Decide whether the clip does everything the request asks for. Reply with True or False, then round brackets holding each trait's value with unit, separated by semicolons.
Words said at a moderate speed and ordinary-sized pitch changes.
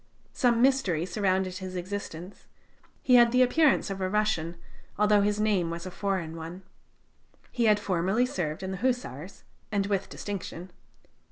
True (155 wpm; 3.0 semitones)